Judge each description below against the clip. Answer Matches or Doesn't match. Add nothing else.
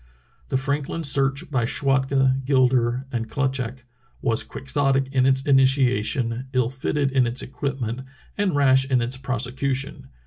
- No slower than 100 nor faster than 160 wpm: Matches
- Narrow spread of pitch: Matches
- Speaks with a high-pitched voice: Doesn't match